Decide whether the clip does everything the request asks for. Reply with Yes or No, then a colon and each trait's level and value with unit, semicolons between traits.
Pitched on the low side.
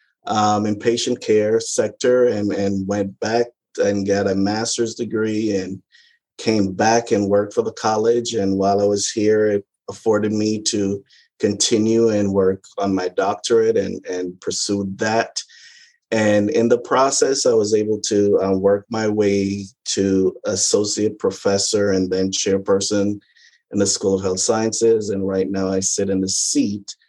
Yes: low, 105 Hz